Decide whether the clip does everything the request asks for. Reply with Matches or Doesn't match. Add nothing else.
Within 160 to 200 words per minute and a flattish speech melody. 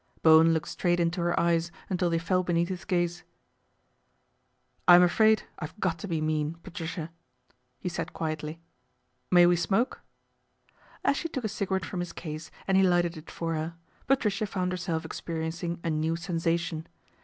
Matches